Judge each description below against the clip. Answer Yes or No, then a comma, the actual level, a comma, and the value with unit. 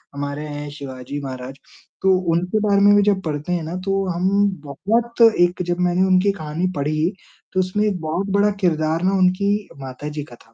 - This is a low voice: No, medium, 175 Hz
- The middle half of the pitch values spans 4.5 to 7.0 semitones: Yes, average, 4.9 semitones